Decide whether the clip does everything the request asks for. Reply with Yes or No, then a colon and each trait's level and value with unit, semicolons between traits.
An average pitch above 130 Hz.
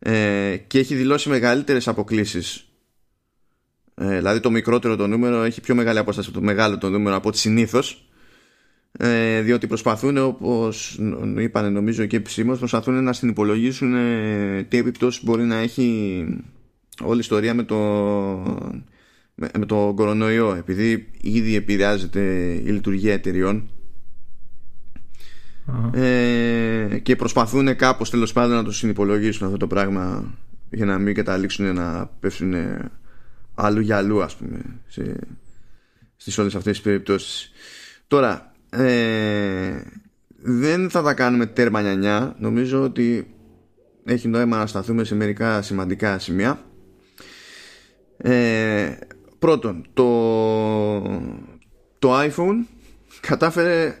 No: low, 110 Hz